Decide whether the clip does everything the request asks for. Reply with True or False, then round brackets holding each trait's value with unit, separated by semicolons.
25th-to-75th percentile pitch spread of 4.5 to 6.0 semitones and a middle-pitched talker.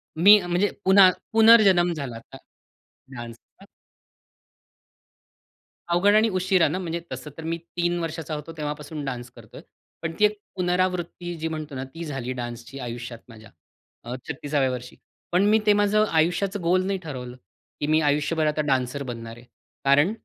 True (5.4 semitones; 160 Hz)